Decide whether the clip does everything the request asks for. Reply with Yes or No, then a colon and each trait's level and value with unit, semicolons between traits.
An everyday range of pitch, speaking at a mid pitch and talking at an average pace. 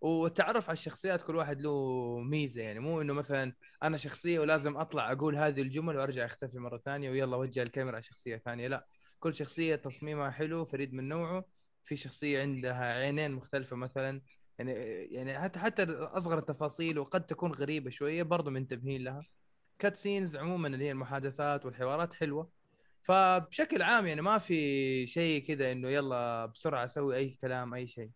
No: average, 3.7 semitones; medium, 145 Hz; fast, 165 wpm